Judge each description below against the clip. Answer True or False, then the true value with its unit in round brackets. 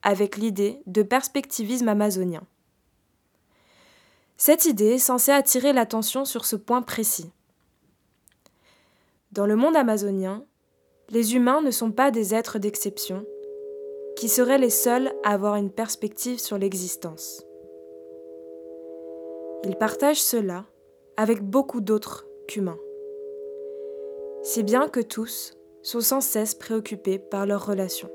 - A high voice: True (220 Hz)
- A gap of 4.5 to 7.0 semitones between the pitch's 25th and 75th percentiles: True (5.2 semitones)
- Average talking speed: False (115 wpm)